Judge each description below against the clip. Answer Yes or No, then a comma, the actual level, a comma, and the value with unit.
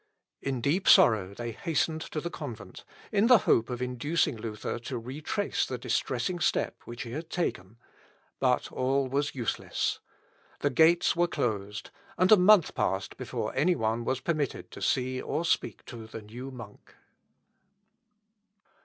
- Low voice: Yes, low, 130 Hz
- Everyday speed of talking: Yes, average, 155 wpm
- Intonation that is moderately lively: No, wide, 5.7 semitones